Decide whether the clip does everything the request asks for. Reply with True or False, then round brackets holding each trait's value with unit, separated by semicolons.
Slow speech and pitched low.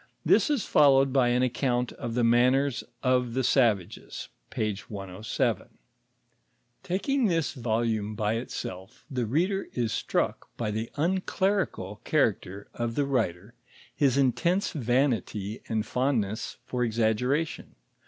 True (125 wpm; 120 Hz)